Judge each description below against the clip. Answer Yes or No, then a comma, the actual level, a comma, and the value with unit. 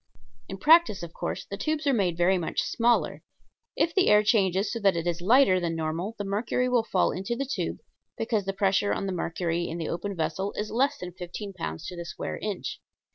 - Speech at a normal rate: No, fast, 220 wpm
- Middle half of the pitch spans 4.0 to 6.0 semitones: Yes, average, 4.6 semitones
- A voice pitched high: Yes, high, 195 Hz